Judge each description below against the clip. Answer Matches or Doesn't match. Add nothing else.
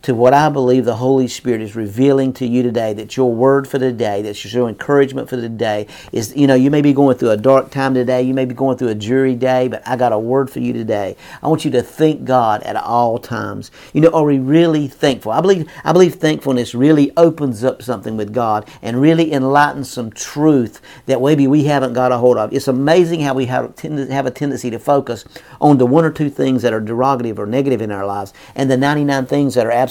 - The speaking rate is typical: Doesn't match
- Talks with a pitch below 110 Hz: Doesn't match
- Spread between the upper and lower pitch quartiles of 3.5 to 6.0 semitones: Doesn't match